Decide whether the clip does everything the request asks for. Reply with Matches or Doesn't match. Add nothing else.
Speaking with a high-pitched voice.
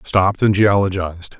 Doesn't match